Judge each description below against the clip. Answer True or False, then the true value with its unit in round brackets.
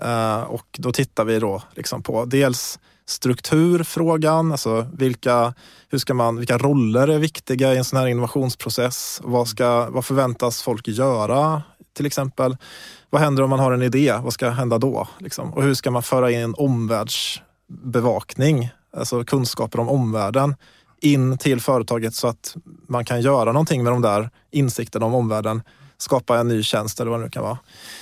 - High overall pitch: False (125 Hz)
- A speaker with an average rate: True (170 wpm)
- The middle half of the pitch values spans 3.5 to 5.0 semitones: False (2.9 semitones)